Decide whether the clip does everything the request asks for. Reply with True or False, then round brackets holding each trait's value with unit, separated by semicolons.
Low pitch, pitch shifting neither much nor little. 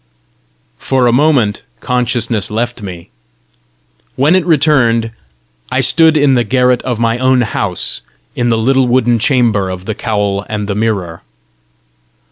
True (120 Hz; 3.5 semitones)